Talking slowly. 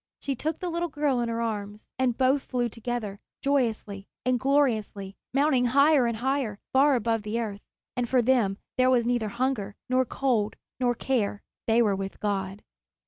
No: average, 175 wpm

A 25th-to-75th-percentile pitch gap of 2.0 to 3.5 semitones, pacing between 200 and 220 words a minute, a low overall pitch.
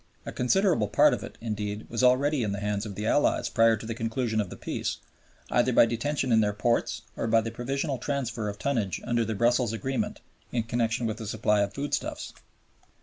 Yes: average, 2.8 semitones; fast, 205 wpm; low, 115 Hz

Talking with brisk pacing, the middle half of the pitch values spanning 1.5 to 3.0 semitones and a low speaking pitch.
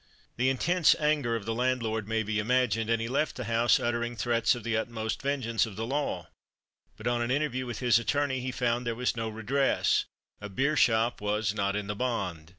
Yes: fast, 210 wpm; narrow, 2.4 semitones; low, 120 Hz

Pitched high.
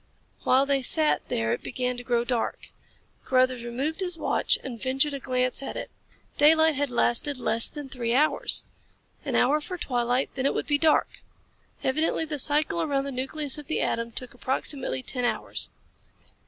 Yes: very high, 265 Hz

